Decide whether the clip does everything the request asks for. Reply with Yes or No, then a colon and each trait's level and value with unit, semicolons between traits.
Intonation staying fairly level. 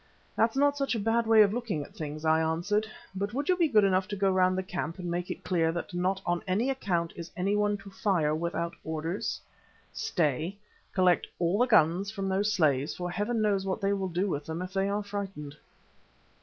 No: average, 3.4 semitones